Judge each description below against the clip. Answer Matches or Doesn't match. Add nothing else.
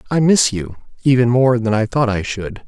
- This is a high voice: Doesn't match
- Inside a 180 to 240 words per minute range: Matches